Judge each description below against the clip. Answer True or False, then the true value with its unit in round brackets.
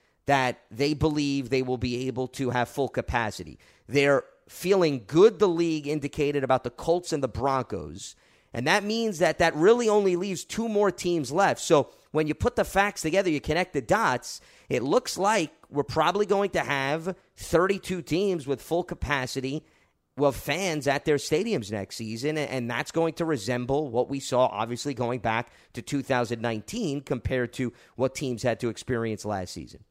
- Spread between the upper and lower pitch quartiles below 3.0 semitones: False (5.2 semitones)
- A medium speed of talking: True (175 wpm)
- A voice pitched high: False (140 Hz)